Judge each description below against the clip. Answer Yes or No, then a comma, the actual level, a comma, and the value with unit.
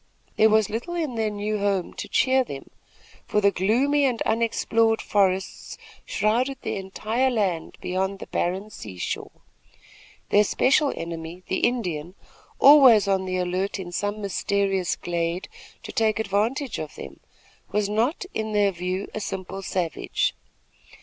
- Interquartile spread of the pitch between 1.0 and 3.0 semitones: No, average, 3.4 semitones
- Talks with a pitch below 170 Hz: No, high, 205 Hz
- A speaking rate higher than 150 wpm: No, average, 145 wpm